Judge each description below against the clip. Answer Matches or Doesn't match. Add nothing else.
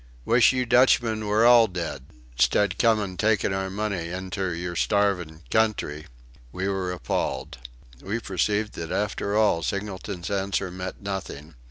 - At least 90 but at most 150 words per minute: Matches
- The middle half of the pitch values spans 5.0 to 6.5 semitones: Doesn't match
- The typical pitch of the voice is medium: Doesn't match